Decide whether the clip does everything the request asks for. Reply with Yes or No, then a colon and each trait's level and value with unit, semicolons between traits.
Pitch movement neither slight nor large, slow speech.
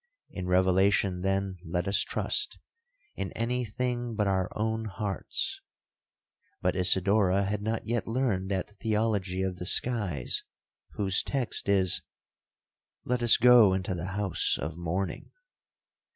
Yes: average, 3.3 semitones; slow, 125 wpm